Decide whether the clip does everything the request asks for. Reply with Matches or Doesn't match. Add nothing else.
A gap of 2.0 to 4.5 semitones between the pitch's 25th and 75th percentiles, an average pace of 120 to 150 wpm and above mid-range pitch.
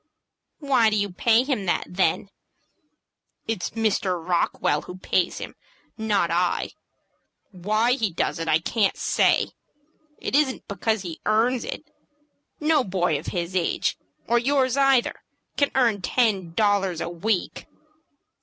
Doesn't match